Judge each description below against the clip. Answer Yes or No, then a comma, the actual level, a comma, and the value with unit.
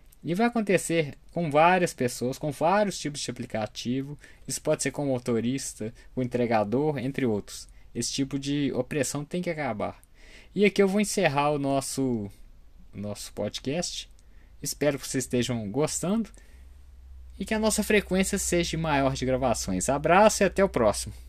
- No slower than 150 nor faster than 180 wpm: Yes, average, 160 wpm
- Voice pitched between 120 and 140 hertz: Yes, low, 135 Hz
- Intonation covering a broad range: Yes, wide, 6.2 semitones